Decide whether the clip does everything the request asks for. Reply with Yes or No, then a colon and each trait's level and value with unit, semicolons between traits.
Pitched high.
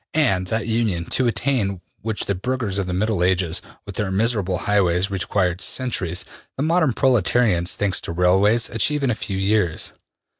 No: low, 100 Hz